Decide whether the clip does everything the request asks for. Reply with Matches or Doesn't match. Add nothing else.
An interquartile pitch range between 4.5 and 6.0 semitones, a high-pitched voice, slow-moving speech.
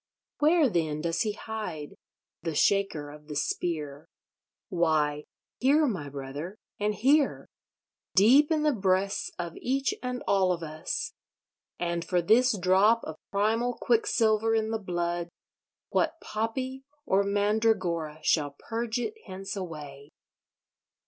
Matches